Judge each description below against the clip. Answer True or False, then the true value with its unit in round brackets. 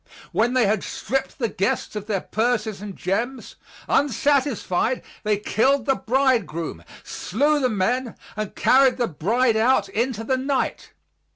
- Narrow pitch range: False (4.0 semitones)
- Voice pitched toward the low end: False (230 Hz)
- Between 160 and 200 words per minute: False (145 wpm)